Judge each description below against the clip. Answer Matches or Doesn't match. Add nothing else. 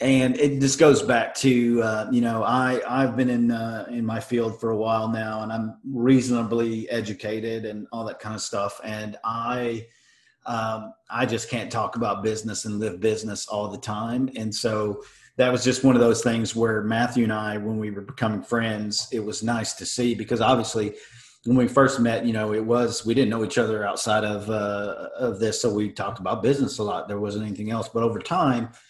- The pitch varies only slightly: Matches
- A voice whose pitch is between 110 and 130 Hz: Matches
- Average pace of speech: Doesn't match